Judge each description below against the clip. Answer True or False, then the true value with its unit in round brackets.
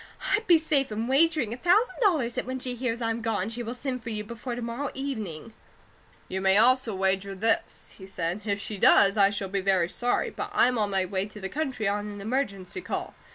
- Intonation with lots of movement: False (4.5 semitones)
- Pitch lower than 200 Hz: False (225 Hz)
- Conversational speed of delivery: False (225 wpm)